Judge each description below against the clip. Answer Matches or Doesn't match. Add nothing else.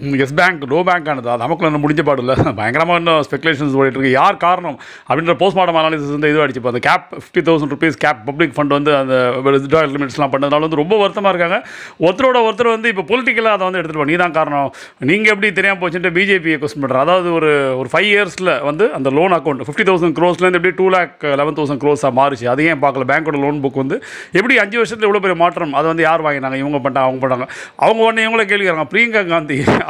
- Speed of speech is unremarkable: Doesn't match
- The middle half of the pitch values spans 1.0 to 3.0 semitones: Doesn't match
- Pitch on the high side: Doesn't match